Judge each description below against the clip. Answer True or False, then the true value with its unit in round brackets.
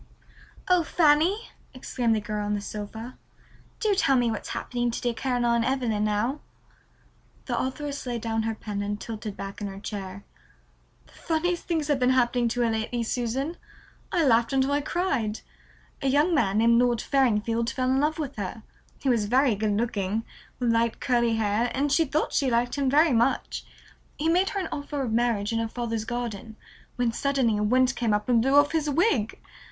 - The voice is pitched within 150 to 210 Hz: False (240 Hz)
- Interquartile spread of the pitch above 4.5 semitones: False (4.0 semitones)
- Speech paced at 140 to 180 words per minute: False (190 wpm)